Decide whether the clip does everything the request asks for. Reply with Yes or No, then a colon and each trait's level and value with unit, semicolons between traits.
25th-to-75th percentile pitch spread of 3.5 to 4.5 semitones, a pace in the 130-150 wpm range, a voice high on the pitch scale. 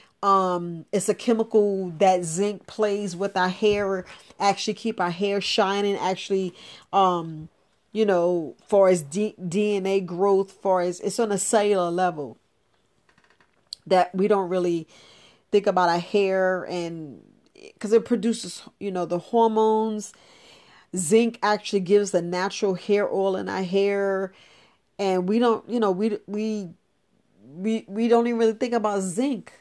No: narrow, 2.6 semitones; average, 145 wpm; high, 195 Hz